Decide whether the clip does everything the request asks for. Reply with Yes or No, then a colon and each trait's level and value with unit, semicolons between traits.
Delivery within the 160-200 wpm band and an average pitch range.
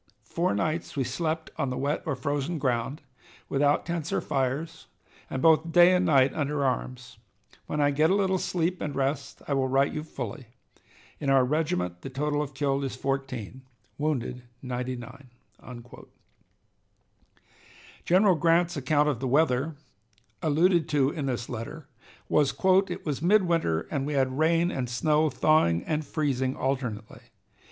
No: average, 150 wpm; average, 3.3 semitones